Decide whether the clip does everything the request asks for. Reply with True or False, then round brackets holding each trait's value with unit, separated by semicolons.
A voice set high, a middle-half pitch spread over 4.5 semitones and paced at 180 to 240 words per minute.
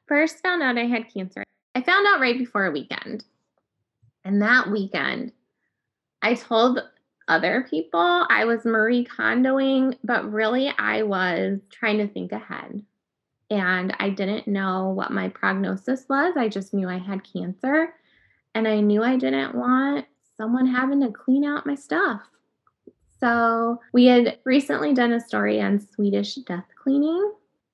False (230 Hz; 4.9 semitones; 150 wpm)